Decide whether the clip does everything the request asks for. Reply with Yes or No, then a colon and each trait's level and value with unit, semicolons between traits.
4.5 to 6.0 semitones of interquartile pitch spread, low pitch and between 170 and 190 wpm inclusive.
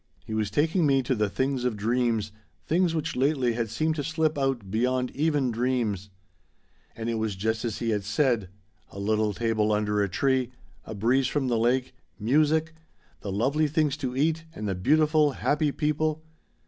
Yes: average, 5.3 semitones; low, 125 Hz; average, 175 wpm